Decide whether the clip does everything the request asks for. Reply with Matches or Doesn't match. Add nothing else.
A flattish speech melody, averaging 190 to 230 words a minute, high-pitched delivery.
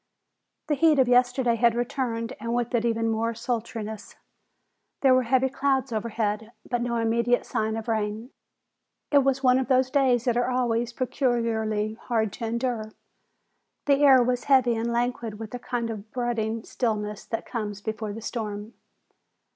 Doesn't match